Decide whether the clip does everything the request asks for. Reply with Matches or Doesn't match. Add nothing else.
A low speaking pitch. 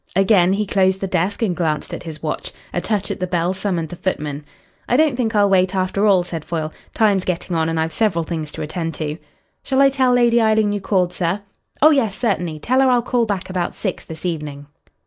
Doesn't match